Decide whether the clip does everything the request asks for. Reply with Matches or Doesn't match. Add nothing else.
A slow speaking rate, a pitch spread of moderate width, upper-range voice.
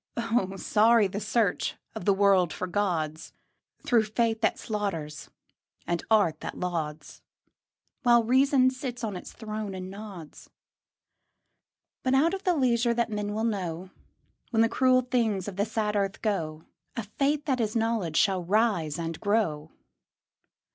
Doesn't match